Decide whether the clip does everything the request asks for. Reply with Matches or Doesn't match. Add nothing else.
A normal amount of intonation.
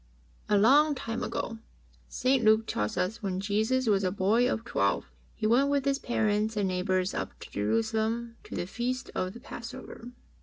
Matches